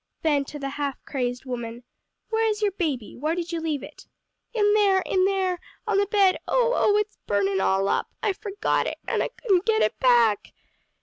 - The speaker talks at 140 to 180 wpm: No, average, 195 wpm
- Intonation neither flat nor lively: No, wide, 8.3 semitones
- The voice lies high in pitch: Yes, very high, 345 Hz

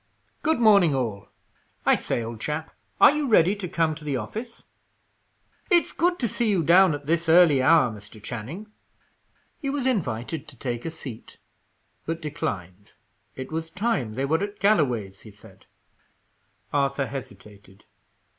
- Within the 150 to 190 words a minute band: Yes, average, 155 wpm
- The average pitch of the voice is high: No, medium, 150 Hz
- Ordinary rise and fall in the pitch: No, wide, 8.5 semitones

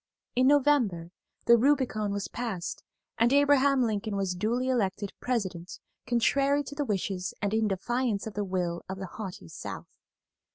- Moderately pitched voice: No, high, 220 Hz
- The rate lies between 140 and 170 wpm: Yes, average, 155 wpm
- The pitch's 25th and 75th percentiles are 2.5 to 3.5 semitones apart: No, average, 5.1 semitones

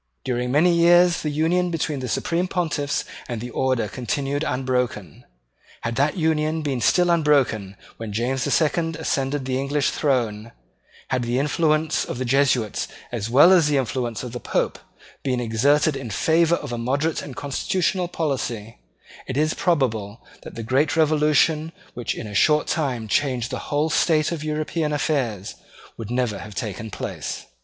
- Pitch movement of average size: Yes, average, 4.4 semitones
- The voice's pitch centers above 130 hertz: Yes, medium, 140 Hz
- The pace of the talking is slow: No, average, 165 wpm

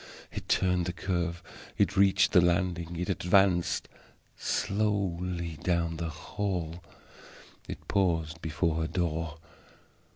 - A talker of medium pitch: No, very low, 85 Hz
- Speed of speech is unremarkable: No, slow, 110 wpm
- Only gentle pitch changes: Yes, narrow, 1.9 semitones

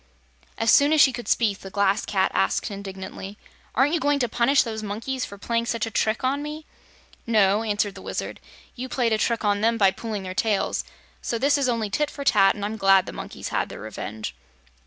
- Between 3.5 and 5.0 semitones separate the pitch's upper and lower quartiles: Yes, average, 4.1 semitones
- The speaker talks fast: Yes, fast, 220 wpm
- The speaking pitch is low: No, high, 220 Hz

